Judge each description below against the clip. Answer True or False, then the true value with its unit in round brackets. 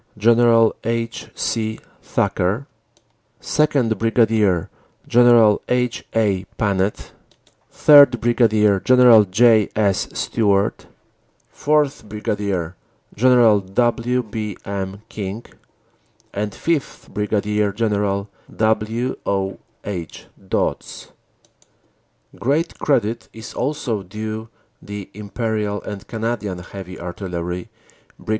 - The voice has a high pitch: False (110 Hz)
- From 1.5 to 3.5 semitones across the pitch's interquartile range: True (2.9 semitones)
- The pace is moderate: False (90 wpm)